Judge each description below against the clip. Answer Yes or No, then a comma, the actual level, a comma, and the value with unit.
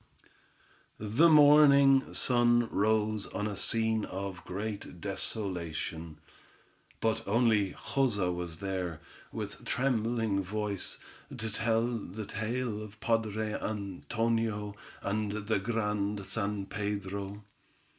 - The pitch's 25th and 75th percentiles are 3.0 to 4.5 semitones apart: No, narrow, 2.4 semitones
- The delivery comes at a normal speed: No, slow, 105 wpm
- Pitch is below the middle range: Yes, low, 105 Hz